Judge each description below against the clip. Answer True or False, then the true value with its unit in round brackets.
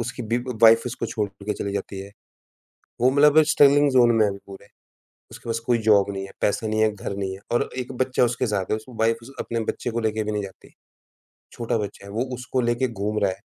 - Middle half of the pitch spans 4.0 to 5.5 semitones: False (3.2 semitones)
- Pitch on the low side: True (115 Hz)